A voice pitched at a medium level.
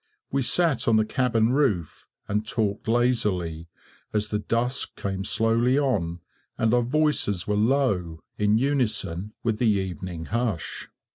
No: low, 110 Hz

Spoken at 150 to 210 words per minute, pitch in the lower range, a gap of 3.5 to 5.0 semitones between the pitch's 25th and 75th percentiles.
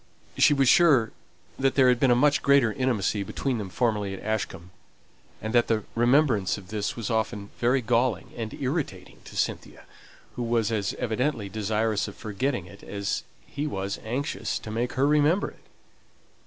Yes: average, 170 wpm; low, 115 Hz; average, 4.2 semitones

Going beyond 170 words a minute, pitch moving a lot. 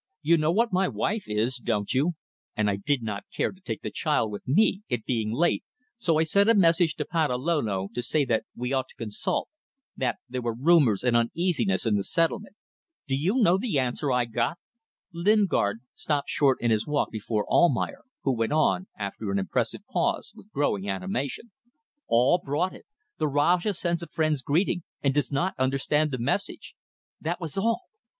Yes: average, 185 wpm; wide, 6.6 semitones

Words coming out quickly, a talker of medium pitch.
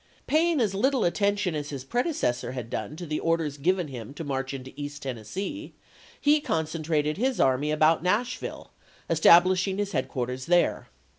No: average, 160 wpm; medium, 160 Hz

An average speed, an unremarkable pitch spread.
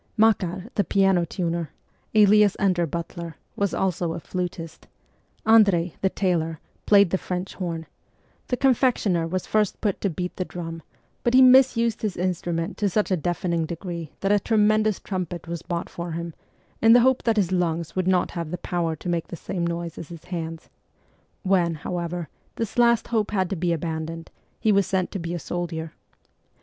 Yes: average, 180 wpm; average, 3.2 semitones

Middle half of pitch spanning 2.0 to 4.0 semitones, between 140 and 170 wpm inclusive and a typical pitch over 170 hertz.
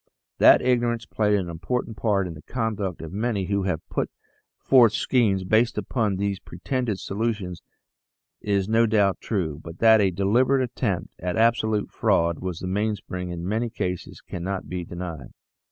No: average, 3.7 semitones; average, 160 wpm; low, 100 Hz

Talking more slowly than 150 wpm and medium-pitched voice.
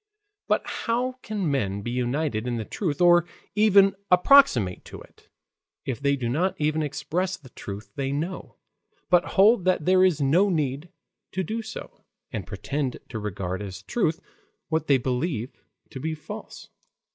No: average, 160 wpm; medium, 155 Hz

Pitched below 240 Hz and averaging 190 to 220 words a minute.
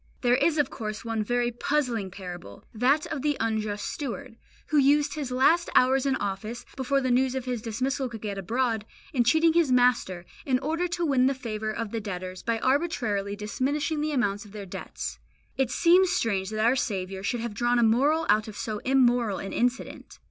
No: high, 245 Hz; average, 200 wpm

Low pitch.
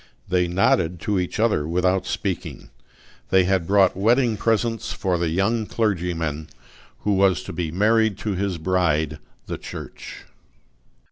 Yes: very low, 95 Hz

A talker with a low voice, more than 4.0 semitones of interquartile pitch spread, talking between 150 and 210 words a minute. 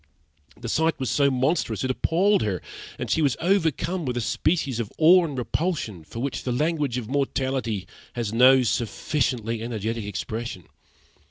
Yes: low, 130 Hz; average, 5.2 semitones; average, 160 wpm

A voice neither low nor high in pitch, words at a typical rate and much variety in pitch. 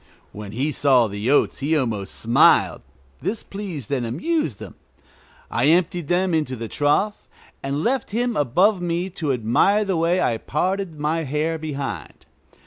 Yes: medium, 155 Hz; average, 155 wpm; wide, 6.0 semitones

